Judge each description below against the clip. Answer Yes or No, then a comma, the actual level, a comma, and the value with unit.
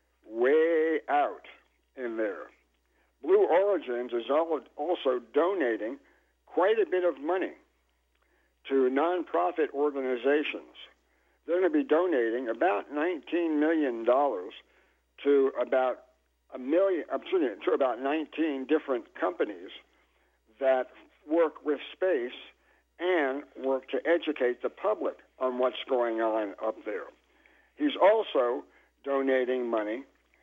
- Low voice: No, medium, 145 Hz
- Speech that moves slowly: Yes, slow, 110 wpm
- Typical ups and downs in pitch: No, wide, 5.7 semitones